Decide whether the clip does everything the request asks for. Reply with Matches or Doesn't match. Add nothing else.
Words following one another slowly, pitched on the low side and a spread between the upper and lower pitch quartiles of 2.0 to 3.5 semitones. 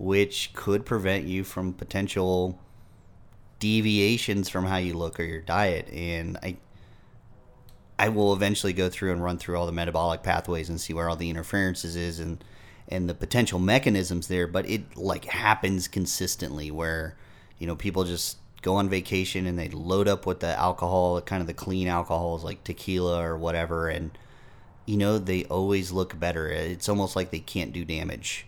Doesn't match